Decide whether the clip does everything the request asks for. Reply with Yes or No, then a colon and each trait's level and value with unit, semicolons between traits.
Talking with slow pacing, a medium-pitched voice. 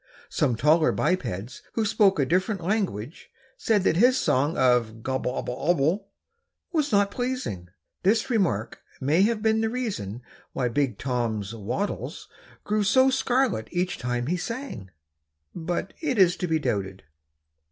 No: average, 145 wpm; medium, 175 Hz